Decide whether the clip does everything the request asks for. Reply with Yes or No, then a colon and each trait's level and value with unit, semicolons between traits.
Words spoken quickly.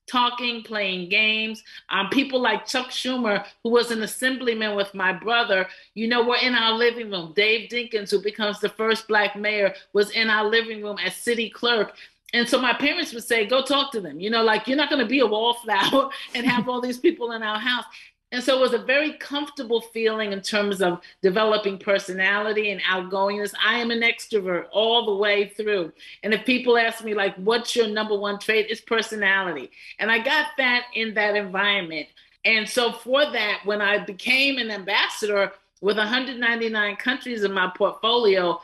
No: average, 195 wpm